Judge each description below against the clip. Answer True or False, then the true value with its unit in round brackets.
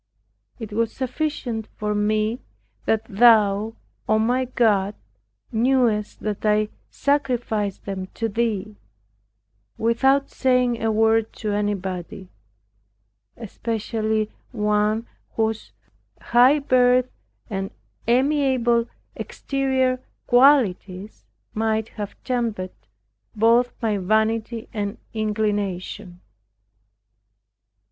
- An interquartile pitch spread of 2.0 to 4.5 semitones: True (2.7 semitones)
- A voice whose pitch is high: True (220 Hz)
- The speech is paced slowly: True (85 wpm)